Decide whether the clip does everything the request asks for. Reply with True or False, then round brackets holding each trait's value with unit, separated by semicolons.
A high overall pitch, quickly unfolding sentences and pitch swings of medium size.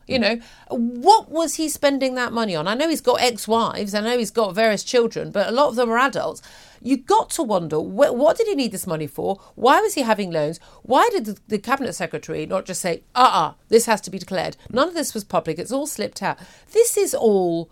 False (230 Hz; 245 wpm; 6.4 semitones)